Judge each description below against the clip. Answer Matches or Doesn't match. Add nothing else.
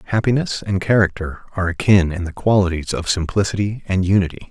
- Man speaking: Matches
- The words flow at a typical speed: Matches